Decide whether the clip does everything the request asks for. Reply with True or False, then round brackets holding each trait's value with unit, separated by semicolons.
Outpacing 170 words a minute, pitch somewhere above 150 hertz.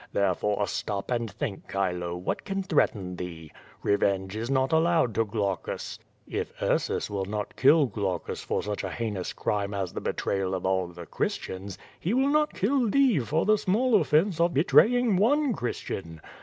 False (185 wpm; 110 Hz)